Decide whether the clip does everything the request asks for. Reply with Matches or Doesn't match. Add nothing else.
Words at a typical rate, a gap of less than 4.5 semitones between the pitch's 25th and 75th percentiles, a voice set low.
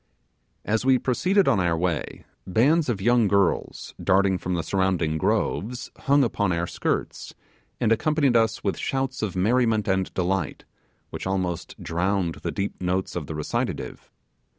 Doesn't match